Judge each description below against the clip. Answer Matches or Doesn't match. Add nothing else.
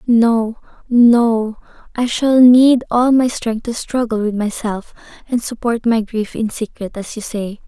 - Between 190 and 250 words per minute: Doesn't match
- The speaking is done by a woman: Matches